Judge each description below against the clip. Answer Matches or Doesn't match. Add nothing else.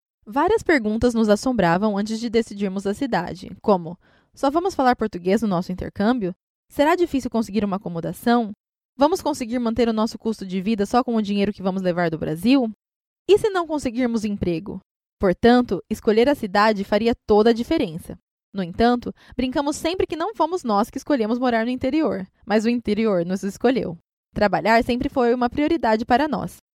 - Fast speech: Doesn't match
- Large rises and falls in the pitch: Doesn't match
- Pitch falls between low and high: Doesn't match